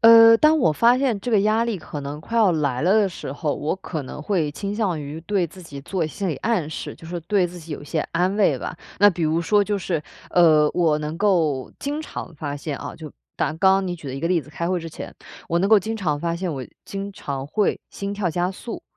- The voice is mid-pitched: Yes, medium, 175 Hz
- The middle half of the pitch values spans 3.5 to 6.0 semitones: Yes, average, 4.8 semitones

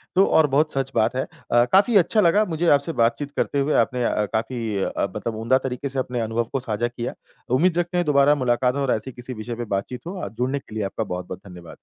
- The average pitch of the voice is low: Yes, low, 125 Hz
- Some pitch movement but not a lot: Yes, average, 4.4 semitones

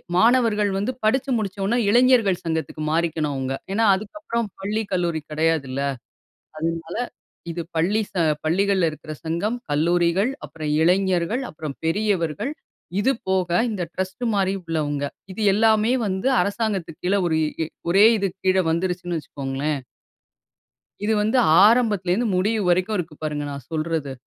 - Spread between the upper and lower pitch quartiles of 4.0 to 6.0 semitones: Yes, average, 4.8 semitones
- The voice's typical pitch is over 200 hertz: No, medium, 185 Hz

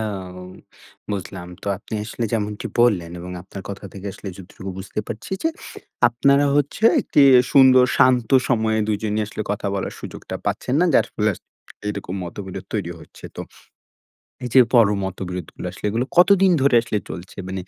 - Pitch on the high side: No, low, 105 Hz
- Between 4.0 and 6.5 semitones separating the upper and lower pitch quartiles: Yes, average, 4.5 semitones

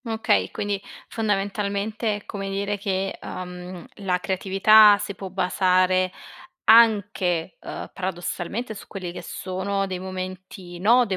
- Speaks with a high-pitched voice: Yes, high, 195 Hz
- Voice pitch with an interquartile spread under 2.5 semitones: Yes, narrow, 1.9 semitones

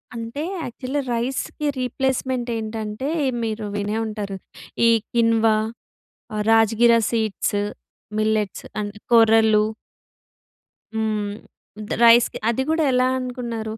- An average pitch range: No, narrow, 2.3 semitones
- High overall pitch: Yes, high, 225 Hz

